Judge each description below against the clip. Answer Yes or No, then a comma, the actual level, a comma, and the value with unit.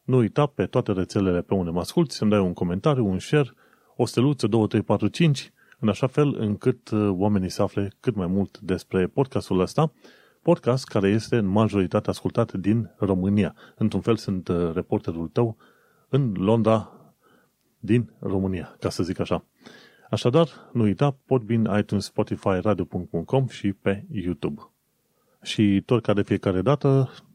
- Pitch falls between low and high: No, low, 105 Hz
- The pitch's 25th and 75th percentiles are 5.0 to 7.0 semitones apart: No, average, 4.0 semitones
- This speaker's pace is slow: No, average, 160 wpm